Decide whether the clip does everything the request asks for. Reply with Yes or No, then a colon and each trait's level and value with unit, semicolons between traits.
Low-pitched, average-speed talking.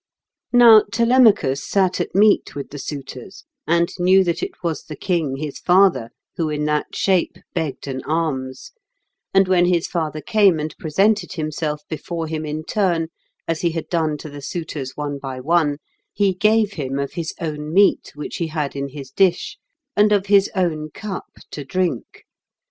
No: medium, 165 Hz; average, 175 wpm